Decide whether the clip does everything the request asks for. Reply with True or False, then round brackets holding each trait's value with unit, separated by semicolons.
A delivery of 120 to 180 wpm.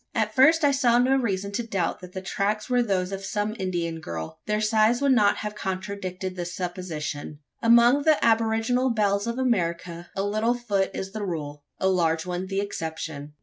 False (190 wpm)